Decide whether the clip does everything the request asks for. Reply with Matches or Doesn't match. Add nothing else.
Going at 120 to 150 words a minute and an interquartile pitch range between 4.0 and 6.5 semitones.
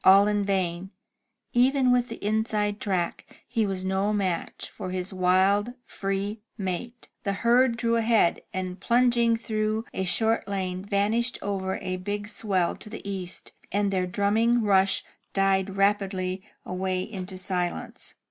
Doesn't match